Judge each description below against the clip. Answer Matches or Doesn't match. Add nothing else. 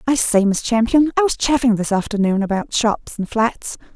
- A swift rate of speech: Doesn't match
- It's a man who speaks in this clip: Doesn't match